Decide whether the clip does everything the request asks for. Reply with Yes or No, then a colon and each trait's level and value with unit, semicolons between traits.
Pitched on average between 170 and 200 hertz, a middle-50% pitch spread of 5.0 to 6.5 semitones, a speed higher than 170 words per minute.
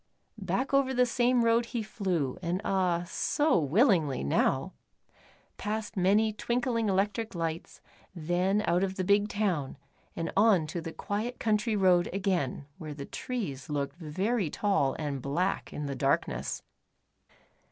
No: high, 190 Hz; average, 5.3 semitones; average, 140 wpm